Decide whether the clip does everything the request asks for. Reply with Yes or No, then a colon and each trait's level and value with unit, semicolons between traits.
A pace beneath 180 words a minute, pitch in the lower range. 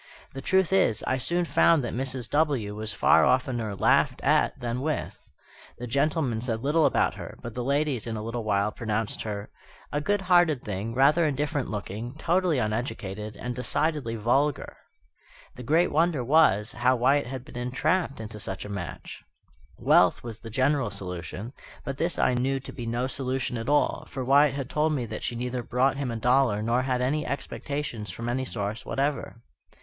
No: average, 185 wpm; low, 125 Hz